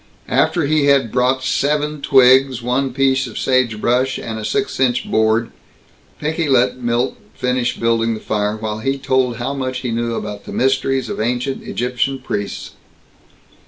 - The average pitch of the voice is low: Yes, low, 125 Hz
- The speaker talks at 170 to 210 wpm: No, average, 160 wpm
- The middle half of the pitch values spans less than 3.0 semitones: Yes, narrow, 2.5 semitones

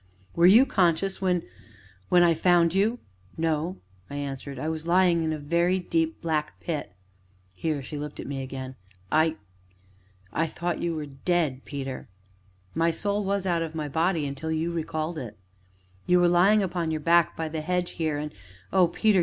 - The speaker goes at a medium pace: Yes, average, 180 wpm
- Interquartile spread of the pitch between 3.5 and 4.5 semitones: No, average, 2.8 semitones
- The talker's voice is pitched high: No, medium, 165 Hz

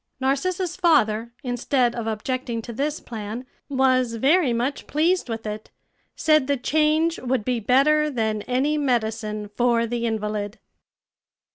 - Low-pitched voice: No, very high, 250 Hz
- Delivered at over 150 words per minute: No, slow, 135 wpm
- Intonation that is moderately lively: Yes, average, 4.4 semitones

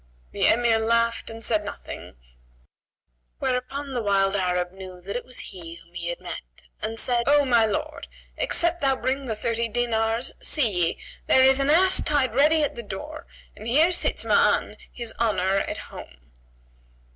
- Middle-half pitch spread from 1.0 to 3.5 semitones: No, average, 5.3 semitones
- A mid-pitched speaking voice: No, high, 230 Hz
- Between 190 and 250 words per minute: No, average, 170 wpm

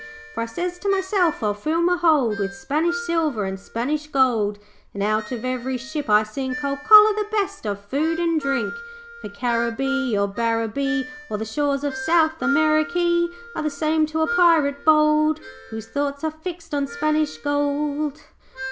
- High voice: Yes, very high, 285 Hz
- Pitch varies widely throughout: Yes, wide, 5.7 semitones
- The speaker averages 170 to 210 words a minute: Yes, average, 175 wpm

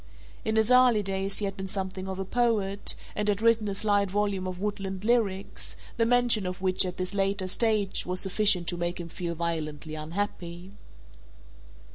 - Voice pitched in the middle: No, high, 195 Hz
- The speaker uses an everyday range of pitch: No, narrow, 2.3 semitones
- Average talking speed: Yes, average, 180 wpm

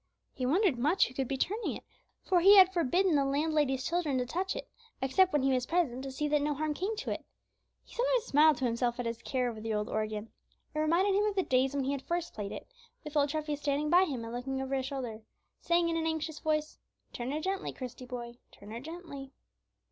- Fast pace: Yes, fast, 240 wpm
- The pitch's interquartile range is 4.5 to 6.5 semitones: Yes, average, 5.1 semitones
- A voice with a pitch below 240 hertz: No, very high, 290 Hz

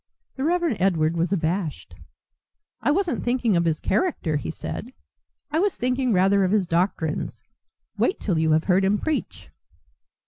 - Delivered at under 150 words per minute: No, average, 160 wpm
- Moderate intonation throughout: No, wide, 7.4 semitones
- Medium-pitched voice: No, high, 195 Hz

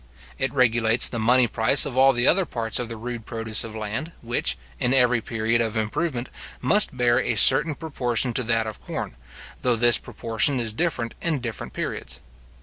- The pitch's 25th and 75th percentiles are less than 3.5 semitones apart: Yes, narrow, 2.4 semitones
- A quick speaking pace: No, average, 185 wpm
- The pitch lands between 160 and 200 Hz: No, low, 120 Hz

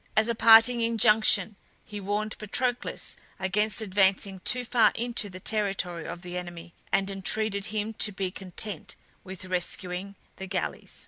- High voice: Yes, high, 200 Hz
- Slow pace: No, average, 145 wpm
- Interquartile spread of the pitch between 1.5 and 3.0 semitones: Yes, average, 2.7 semitones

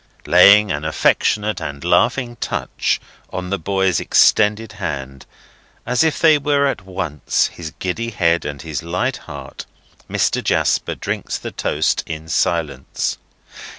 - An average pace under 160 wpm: Yes, slow, 135 wpm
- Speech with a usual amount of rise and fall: No, wide, 5.8 semitones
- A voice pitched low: Yes, very low, 90 Hz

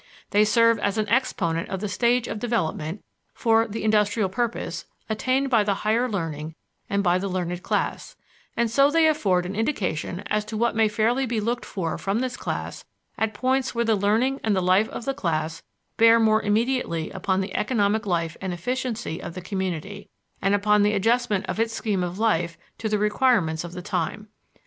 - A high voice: Yes, high, 210 Hz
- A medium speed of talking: Yes, average, 190 wpm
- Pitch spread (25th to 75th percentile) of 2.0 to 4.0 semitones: Yes, average, 3.7 semitones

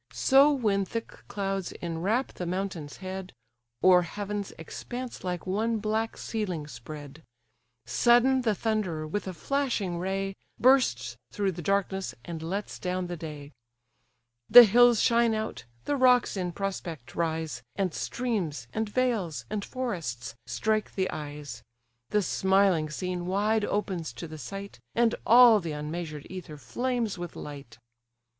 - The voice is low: No, high, 190 Hz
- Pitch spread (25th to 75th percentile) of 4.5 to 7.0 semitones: Yes, average, 5.2 semitones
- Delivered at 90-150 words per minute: Yes, average, 140 wpm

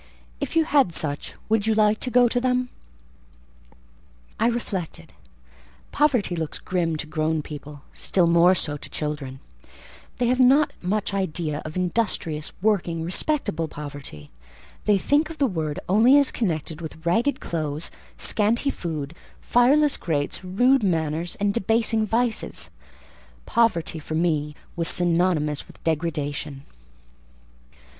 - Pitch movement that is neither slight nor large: No, wide, 6.9 semitones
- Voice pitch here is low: No, medium, 175 Hz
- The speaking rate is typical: No, slow, 130 wpm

